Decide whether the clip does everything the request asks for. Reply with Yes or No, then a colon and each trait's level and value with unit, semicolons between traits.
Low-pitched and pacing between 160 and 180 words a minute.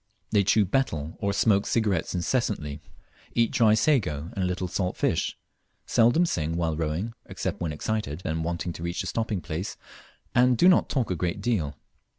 Yes: very low, 95 Hz; average, 175 wpm